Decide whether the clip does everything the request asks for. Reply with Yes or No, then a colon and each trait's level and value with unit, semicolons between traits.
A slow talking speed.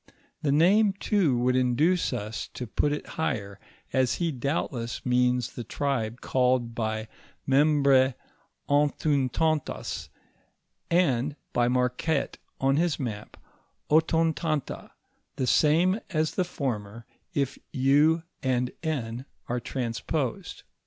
Yes: slow, 110 wpm